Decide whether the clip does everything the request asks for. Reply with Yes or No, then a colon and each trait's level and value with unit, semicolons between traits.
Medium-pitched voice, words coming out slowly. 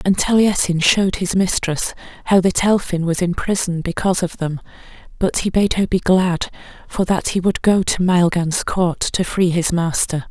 No: medium, 180 Hz; average, 185 wpm